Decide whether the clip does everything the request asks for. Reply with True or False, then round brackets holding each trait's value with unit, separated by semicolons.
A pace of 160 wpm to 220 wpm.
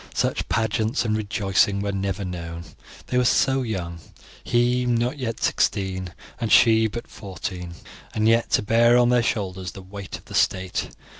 True (165 wpm)